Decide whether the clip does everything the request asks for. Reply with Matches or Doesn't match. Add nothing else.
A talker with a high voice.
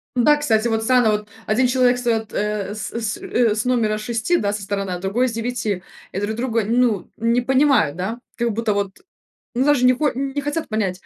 Matches